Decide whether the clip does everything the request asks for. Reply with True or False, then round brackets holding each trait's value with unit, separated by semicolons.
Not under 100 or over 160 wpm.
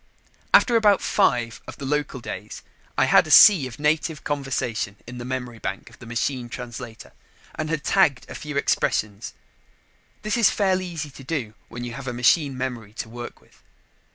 False (180 wpm)